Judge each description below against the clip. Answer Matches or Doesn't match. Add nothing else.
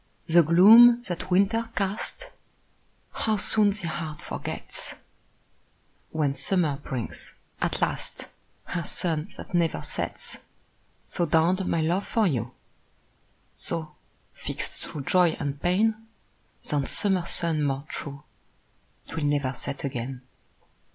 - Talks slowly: Matches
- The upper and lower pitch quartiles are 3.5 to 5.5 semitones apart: Matches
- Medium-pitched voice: Matches